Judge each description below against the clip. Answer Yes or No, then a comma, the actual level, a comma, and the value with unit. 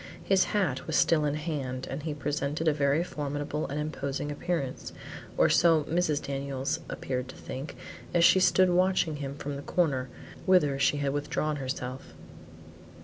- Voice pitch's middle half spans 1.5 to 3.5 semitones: Yes, average, 2.8 semitones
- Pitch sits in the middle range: Yes, medium, 145 Hz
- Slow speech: No, average, 165 wpm